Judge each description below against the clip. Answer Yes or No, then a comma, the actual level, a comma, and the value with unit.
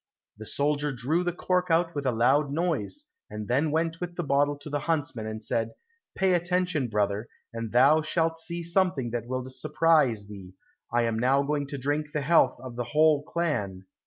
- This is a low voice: No, medium, 145 Hz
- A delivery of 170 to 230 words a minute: Yes, average, 190 wpm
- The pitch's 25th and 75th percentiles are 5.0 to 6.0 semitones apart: Yes, wide, 5.4 semitones